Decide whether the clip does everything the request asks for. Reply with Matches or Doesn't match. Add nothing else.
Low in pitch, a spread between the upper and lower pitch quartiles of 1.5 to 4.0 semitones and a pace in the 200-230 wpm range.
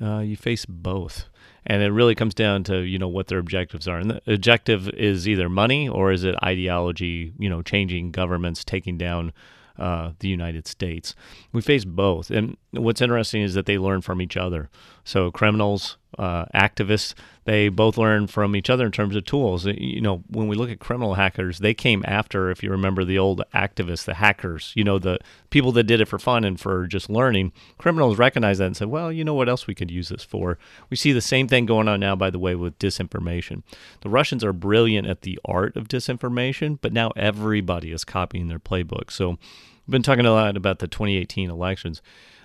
Matches